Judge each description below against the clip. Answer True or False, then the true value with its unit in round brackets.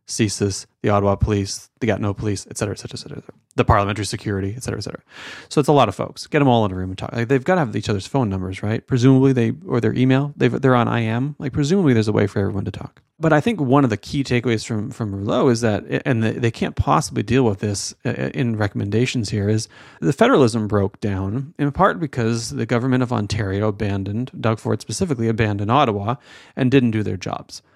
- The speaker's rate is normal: False (240 wpm)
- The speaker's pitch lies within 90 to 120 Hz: True (115 Hz)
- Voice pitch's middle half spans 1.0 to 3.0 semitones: False (3.9 semitones)